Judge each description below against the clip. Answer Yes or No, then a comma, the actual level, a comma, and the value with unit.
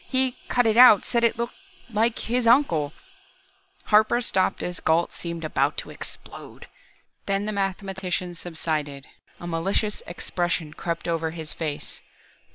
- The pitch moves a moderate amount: No, wide, 5.8 semitones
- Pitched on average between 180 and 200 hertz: Yes, high, 190 Hz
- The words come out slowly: No, average, 150 wpm